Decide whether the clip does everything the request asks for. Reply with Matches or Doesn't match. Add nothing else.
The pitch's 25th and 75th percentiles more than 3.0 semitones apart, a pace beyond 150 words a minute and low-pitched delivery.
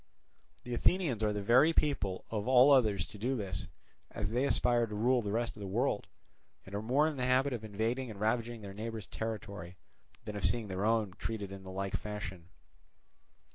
Matches